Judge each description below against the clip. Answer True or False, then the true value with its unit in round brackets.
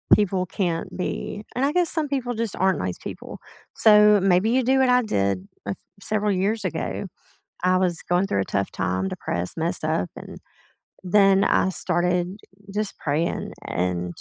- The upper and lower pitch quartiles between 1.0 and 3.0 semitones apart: False (4.7 semitones)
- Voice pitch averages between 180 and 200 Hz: True (185 Hz)